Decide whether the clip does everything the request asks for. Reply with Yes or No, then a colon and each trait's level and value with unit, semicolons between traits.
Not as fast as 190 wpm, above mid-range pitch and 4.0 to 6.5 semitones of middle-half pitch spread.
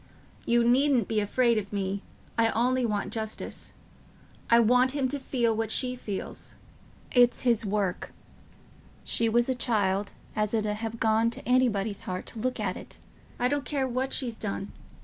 No: average, 170 wpm; high, 230 Hz; average, 3.0 semitones